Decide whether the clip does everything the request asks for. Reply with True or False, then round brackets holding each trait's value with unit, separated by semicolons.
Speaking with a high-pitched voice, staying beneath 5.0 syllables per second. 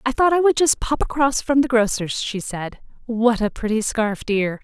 True (235 Hz; 4.7 syllables/s)